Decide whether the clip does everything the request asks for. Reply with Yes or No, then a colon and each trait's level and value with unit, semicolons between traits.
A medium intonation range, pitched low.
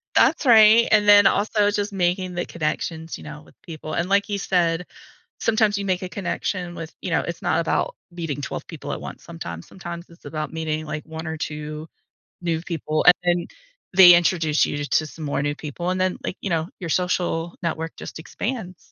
No: average, 3.1 semitones; medium, 175 Hz